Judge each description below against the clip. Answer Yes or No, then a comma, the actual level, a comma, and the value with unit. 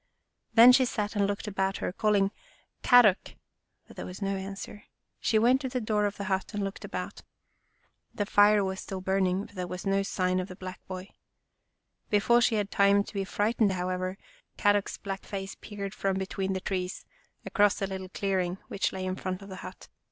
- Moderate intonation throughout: No, narrow, 1.6 semitones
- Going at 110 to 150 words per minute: No, fast, 205 wpm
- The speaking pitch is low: No, high, 195 Hz